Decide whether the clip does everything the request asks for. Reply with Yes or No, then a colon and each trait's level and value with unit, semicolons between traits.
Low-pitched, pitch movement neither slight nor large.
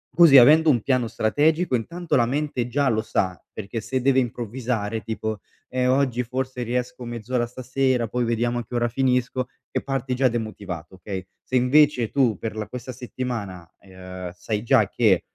Yes: low, 120 Hz; average, 3.0 semitones